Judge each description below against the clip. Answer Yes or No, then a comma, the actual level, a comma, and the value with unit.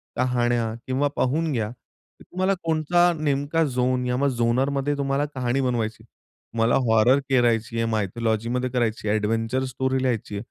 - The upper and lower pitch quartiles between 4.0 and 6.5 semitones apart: No, average, 3.0 semitones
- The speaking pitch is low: Yes, low, 125 Hz